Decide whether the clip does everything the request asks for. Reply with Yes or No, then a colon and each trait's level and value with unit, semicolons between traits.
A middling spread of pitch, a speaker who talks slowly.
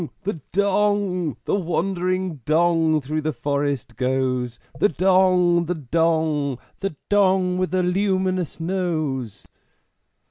Yes: average, 4.1 semitones; slow, 110 wpm